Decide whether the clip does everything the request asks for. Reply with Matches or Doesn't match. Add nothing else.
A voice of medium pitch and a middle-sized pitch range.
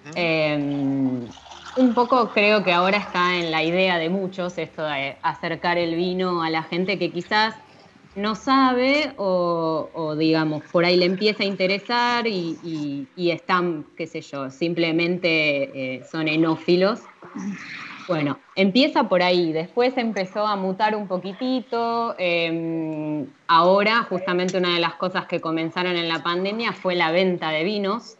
Matches